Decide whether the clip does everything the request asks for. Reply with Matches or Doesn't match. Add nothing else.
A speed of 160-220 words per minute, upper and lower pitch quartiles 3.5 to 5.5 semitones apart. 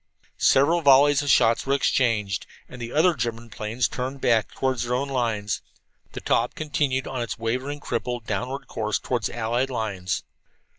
Doesn't match